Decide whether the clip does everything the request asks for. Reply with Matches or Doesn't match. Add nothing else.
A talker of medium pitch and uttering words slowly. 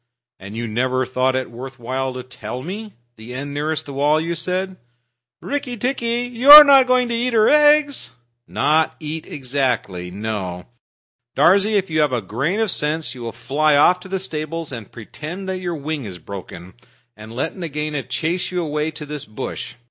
Doesn't match